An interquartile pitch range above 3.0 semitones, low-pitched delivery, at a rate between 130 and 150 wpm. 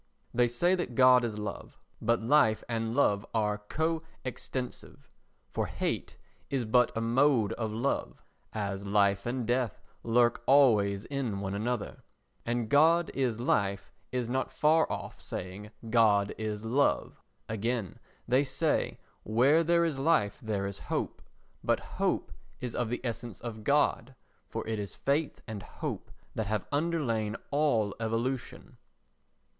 Yes: average, 4.0 semitones; low, 115 Hz; average, 145 wpm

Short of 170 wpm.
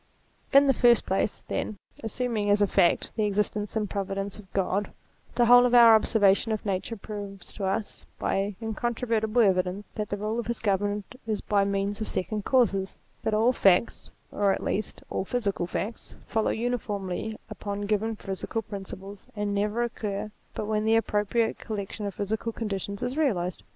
No: average, 175 wpm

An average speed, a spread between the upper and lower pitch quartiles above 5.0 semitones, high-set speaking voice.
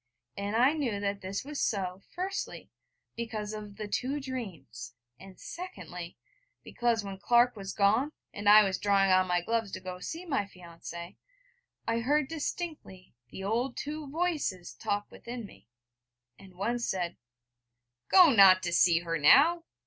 Yes: average, 155 wpm; wide, 5.6 semitones; high, 205 Hz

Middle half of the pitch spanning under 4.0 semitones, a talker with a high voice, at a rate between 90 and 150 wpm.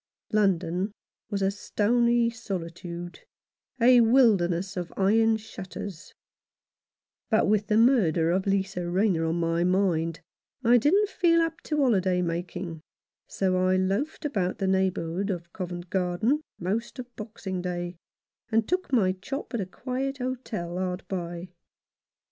No: average, 4.6 semitones; high, 195 Hz; slow, 135 wpm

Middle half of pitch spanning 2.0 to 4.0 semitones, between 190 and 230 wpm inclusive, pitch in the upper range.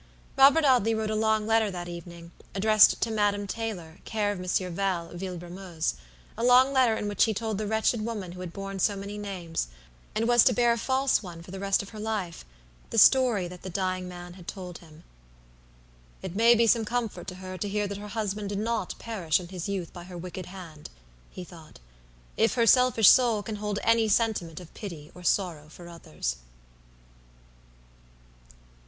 Yes: average, 3.7 semitones; average, 195 wpm; high, 200 Hz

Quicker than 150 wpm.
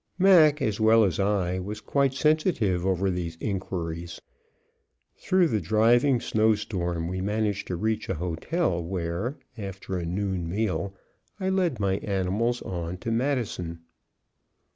No: average, 140 wpm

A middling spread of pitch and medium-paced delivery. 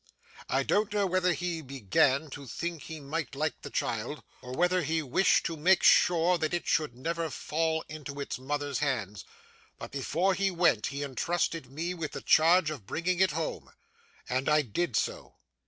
Yes: average, 3.9 semitones; average, 180 wpm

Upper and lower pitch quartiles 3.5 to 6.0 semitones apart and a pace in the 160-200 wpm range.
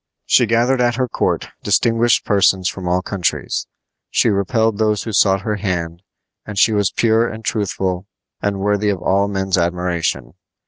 No: average, 3.1 semitones; average, 165 wpm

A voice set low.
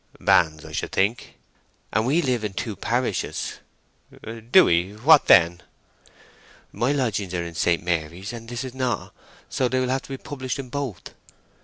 Yes: low, 115 Hz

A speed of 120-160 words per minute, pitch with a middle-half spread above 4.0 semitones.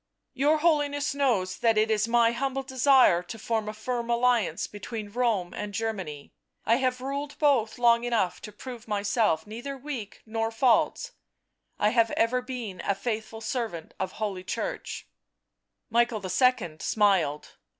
No: average, 155 wpm; average, 3.4 semitones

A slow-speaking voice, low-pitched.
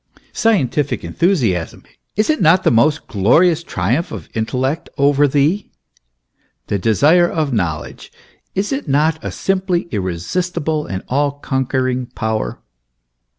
No: slow, 125 wpm; medium, 145 Hz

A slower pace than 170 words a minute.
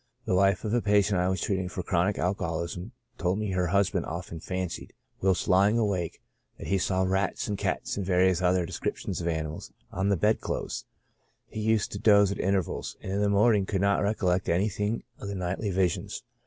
No: average, 200 wpm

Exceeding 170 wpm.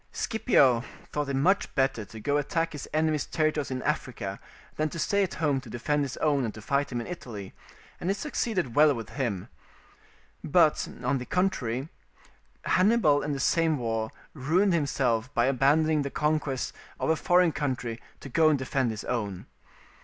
Yes: average, 180 wpm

